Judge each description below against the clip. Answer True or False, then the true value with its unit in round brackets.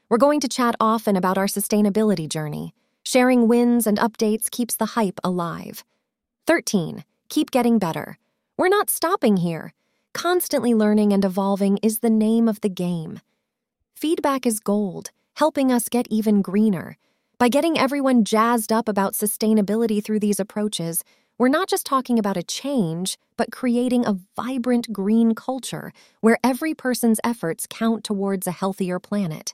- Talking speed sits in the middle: True (150 wpm)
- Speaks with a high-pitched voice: True (220 Hz)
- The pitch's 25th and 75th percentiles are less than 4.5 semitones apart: True (3.6 semitones)